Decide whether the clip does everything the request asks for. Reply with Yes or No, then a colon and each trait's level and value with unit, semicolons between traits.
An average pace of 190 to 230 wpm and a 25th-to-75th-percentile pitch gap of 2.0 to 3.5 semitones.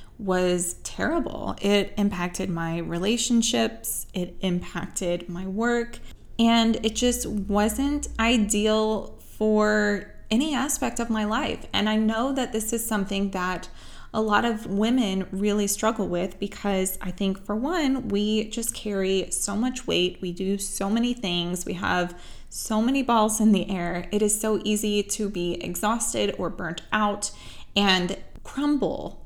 No: average, 150 wpm; average, 3.2 semitones